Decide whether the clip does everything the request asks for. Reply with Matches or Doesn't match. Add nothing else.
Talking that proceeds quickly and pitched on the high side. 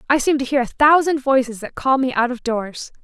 Matches